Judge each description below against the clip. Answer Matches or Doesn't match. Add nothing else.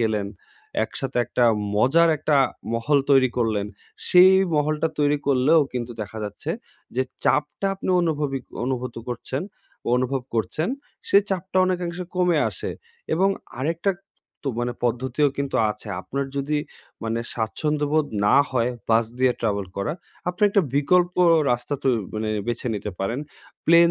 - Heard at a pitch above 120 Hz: Matches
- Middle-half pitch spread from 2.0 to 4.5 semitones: Doesn't match